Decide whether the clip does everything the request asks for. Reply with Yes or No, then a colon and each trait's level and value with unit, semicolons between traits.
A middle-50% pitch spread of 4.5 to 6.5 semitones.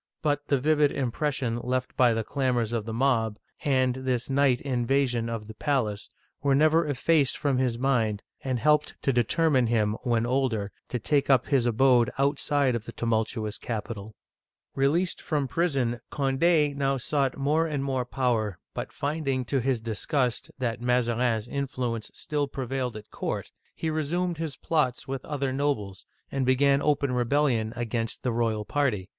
No: average, 3.4 semitones